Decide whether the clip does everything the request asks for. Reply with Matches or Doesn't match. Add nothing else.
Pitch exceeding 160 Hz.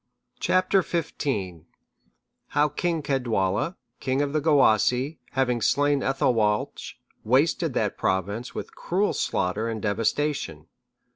Doesn't match